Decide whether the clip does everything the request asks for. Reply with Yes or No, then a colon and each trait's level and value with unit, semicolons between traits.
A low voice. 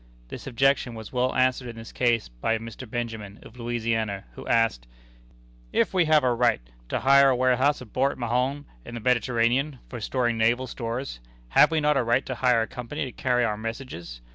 Yes: low, 120 Hz